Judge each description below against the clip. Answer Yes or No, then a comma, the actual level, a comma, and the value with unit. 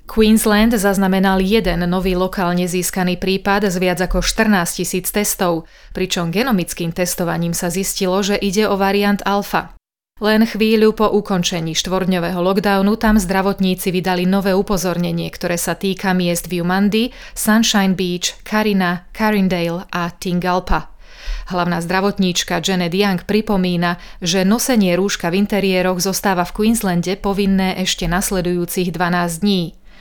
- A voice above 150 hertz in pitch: Yes, high, 190 Hz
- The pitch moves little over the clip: Yes, narrow, 2.2 semitones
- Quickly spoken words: No, average, 125 wpm